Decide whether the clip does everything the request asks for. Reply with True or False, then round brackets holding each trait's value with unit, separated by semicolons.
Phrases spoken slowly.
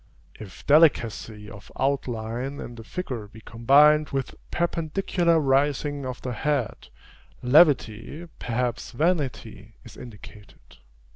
True (110 wpm)